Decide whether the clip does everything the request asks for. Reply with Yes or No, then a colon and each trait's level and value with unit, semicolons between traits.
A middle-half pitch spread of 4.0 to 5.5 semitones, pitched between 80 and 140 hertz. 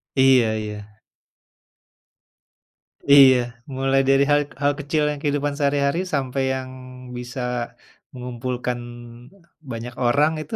No: narrow, 2.6 semitones; low, 135 Hz